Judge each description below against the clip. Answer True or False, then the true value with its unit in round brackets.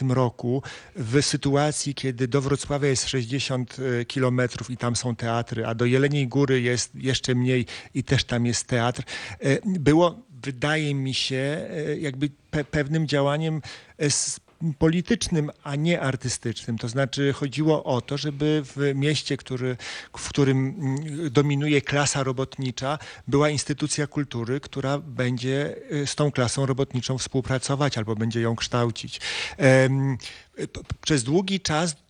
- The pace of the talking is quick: False (130 wpm)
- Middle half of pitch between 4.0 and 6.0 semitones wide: False (2.7 semitones)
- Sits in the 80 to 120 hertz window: False (135 Hz)